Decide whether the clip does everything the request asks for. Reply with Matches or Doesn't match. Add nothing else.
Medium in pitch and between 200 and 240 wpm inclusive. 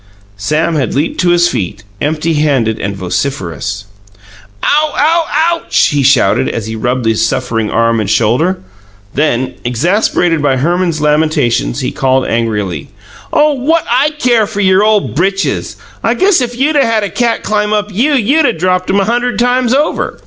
Doesn't match